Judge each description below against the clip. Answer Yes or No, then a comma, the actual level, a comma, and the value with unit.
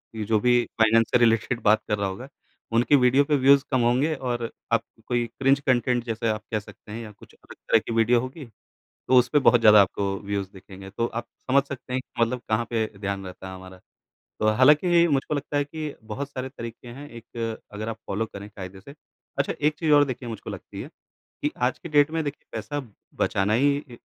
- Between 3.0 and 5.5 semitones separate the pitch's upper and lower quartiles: Yes, average, 4.3 semitones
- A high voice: No, low, 120 Hz